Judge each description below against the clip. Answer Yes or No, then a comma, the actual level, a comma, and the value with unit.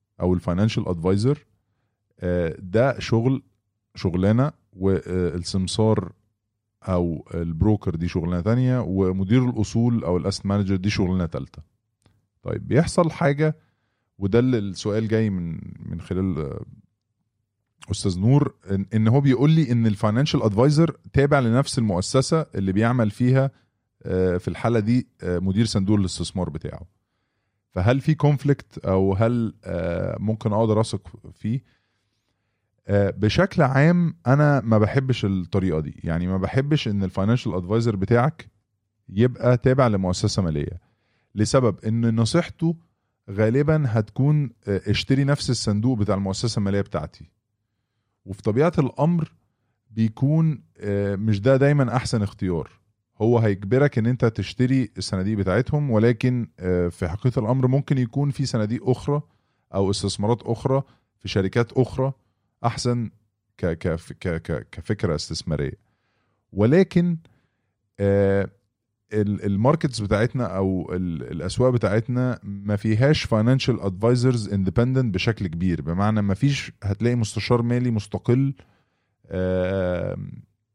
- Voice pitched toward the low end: Yes, low, 110 Hz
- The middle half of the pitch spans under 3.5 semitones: No, average, 4.3 semitones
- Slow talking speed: Yes, slow, 110 wpm